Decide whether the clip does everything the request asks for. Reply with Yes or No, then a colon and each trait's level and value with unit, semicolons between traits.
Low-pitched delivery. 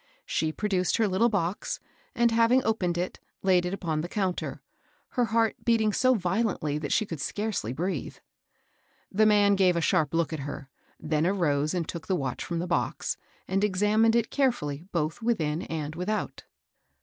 No: medium, 185 Hz